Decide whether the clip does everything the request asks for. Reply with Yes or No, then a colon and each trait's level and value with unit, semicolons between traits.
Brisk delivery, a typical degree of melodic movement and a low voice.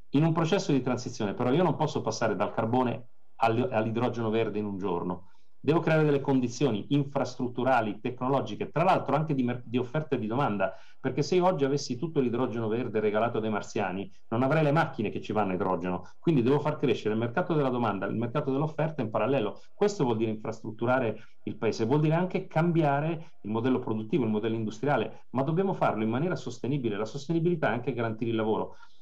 Yes: fast, 195 wpm; average, 4.7 semitones; low, 125 Hz